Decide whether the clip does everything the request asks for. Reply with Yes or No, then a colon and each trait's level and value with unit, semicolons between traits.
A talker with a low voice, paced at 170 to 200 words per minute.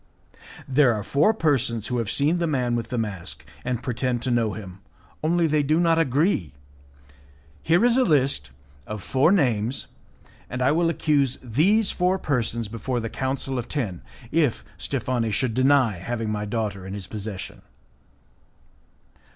No: low, 125 Hz; average, 160 wpm